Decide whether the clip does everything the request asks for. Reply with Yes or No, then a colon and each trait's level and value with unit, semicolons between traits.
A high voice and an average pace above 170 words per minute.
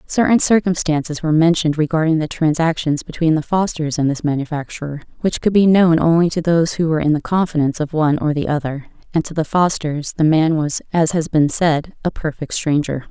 No: medium, 160 Hz; average, 200 wpm